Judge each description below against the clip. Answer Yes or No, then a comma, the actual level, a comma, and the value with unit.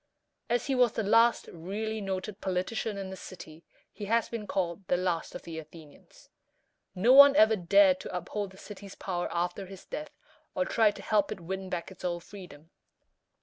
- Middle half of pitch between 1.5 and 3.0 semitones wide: No, average, 3.4 semitones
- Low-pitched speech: No, high, 190 Hz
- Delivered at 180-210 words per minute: Yes, average, 190 wpm